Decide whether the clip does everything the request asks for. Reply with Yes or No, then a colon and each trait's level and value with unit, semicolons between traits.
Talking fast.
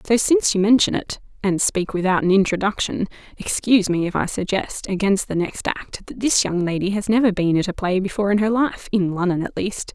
Yes: fast, 215 wpm